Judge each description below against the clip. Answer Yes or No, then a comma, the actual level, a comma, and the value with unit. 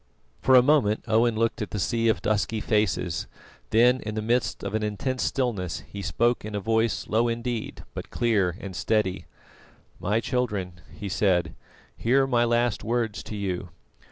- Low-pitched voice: Yes, low, 110 Hz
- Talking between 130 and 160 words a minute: No, average, 170 wpm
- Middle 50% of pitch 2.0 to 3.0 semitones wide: Yes, average, 2.7 semitones